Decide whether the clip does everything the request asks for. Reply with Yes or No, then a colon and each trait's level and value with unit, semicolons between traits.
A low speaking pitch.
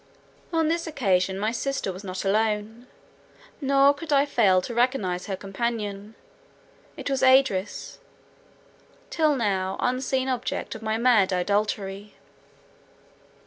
No: high, 225 Hz